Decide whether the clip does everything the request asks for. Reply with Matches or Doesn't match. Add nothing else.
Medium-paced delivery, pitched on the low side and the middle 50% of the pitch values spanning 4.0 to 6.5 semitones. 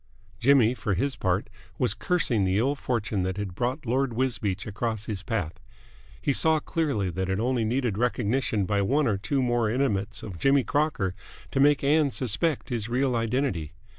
Matches